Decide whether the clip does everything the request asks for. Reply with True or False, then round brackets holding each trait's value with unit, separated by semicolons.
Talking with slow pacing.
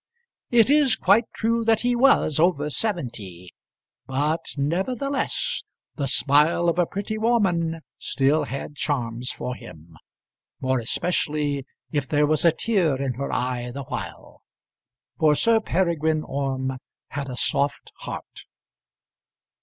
True (130 wpm)